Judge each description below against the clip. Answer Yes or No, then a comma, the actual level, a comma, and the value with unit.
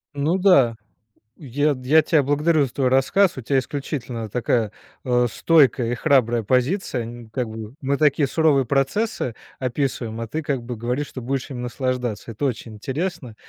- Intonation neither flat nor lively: Yes, average, 3.4 semitones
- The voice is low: Yes, low, 130 Hz